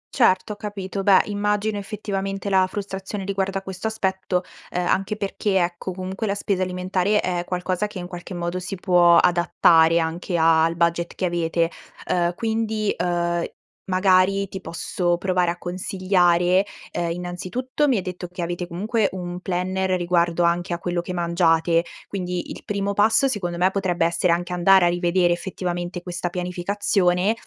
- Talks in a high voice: No, medium, 180 Hz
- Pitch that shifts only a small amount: Yes, narrow, 2.1 semitones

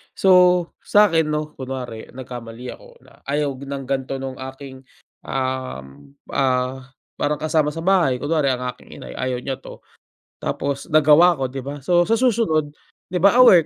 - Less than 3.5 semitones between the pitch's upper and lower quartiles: No, average, 4.0 semitones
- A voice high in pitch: No, medium, 140 Hz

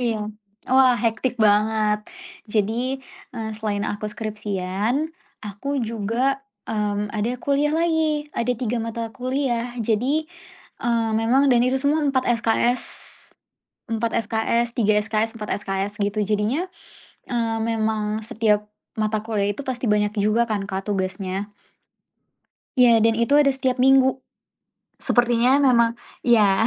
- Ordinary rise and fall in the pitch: Yes, average, 3.1 semitones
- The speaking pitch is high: Yes, high, 225 Hz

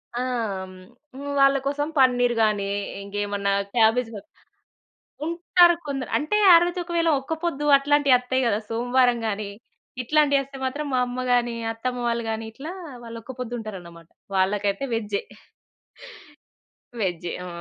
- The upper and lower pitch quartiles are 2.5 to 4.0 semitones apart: No, average, 4.8 semitones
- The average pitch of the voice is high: Yes, high, 245 Hz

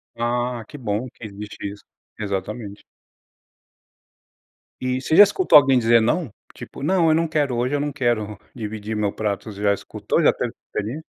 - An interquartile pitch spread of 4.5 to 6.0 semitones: Yes, average, 5.2 semitones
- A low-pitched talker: Yes, low, 120 Hz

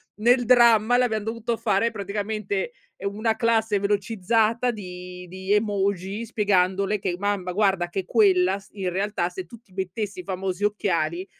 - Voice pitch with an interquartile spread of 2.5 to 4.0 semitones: Yes, average, 2.9 semitones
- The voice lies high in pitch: Yes, high, 205 Hz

